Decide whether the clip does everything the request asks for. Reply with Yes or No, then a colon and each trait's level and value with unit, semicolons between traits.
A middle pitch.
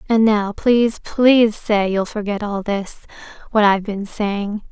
No: high, 210 Hz